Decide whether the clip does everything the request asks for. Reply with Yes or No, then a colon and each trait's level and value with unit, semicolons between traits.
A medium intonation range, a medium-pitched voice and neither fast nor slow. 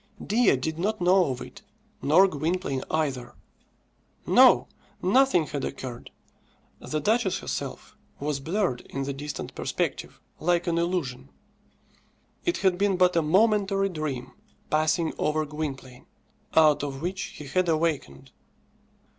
No: average, 4.8 semitones; medium, 160 Hz; slow, 130 wpm